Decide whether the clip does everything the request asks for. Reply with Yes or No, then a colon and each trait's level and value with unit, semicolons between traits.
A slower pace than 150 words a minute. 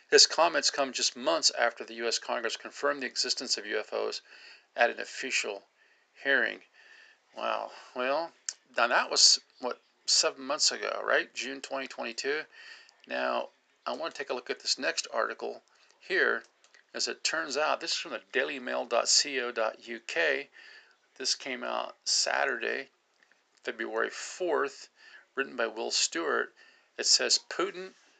Yes: slow, 135 wpm